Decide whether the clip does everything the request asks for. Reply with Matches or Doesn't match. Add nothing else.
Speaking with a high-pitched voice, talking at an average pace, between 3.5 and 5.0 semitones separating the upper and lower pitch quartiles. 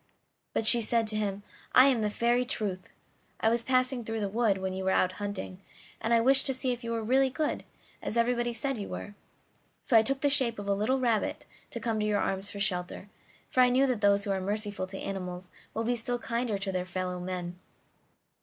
Doesn't match